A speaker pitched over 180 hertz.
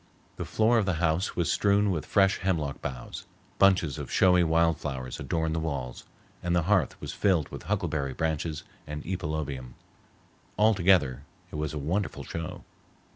No: very low, 80 Hz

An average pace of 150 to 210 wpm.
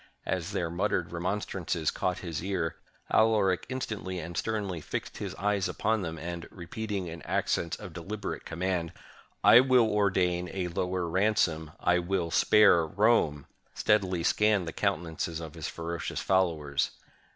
No: average, 140 wpm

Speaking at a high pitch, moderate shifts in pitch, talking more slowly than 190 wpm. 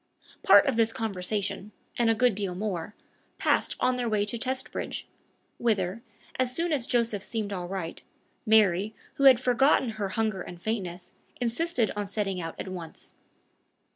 Yes: high, 215 Hz; average, 4.0 semitones; average, 160 wpm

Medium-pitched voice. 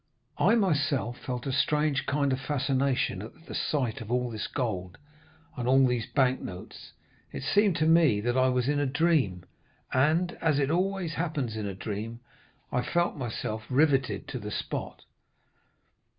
No: low, 130 Hz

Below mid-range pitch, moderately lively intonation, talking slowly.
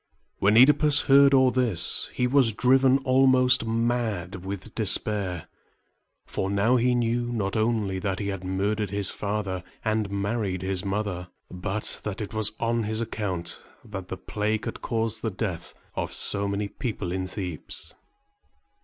No: low, 105 Hz; average, 3.4 semitones; average, 155 wpm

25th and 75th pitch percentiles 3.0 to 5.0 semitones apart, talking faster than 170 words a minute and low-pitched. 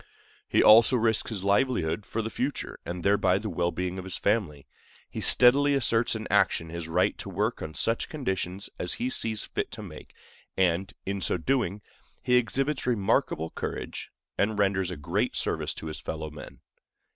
Yes: average, 4.7 semitones; average, 180 wpm; low, 100 Hz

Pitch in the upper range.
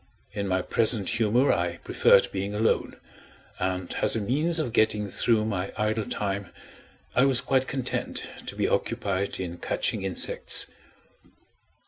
No: low, 105 Hz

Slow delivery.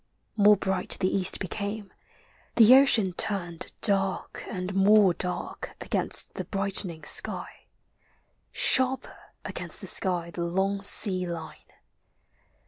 Yes: slow, 120 wpm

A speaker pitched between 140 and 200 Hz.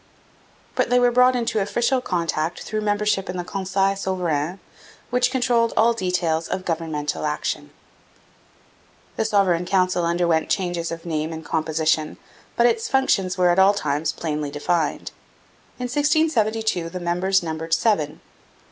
Yes: medium, 185 Hz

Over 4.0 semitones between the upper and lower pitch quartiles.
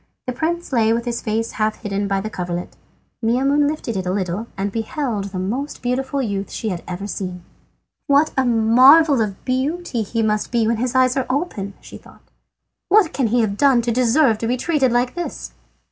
Yes: average, 4.5 semitones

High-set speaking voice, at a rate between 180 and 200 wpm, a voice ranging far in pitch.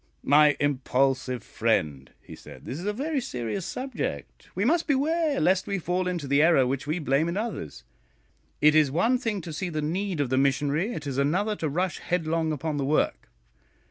No: medium, 160 Hz; average, 195 wpm; wide, 6.0 semitones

